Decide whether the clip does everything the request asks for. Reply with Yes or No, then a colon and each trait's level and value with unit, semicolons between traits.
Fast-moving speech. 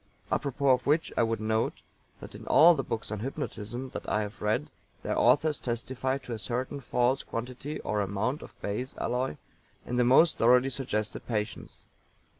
No: average, 175 wpm